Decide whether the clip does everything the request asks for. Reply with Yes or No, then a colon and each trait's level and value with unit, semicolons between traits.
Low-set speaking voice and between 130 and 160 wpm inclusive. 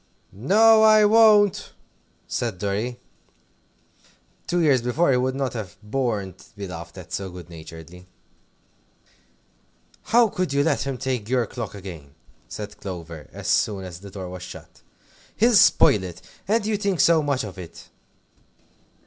Yes: low, 120 Hz; average, 150 wpm